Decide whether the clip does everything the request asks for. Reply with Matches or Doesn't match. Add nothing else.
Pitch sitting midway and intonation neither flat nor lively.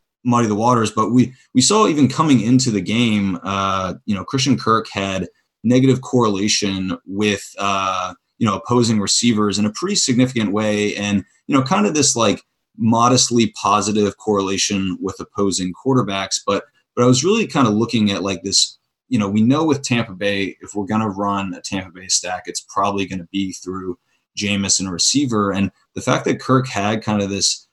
Doesn't match